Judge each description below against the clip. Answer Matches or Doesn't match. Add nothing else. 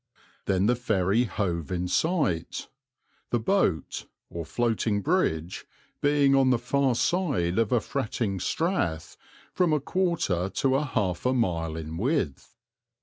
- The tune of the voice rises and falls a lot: Matches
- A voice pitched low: Matches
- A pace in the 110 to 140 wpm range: Matches